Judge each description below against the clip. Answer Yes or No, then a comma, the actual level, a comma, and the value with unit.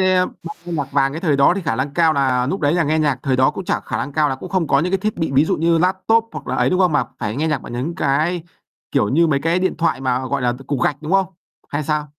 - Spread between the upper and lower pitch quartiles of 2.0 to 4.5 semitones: Yes, average, 4.0 semitones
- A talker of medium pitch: Yes, medium, 150 Hz